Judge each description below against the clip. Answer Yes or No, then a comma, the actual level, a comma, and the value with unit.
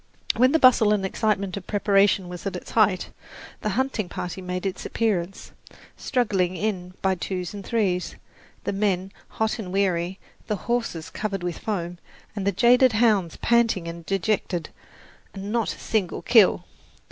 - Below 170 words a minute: Yes, average, 160 wpm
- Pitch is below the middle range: No, high, 195 Hz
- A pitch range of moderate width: Yes, average, 3.2 semitones